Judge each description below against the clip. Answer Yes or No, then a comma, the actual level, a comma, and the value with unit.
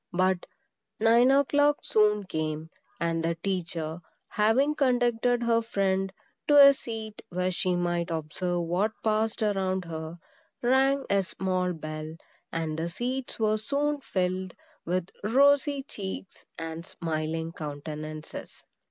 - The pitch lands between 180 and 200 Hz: Yes, high, 190 Hz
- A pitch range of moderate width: No, wide, 6.0 semitones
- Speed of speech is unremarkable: No, slow, 125 wpm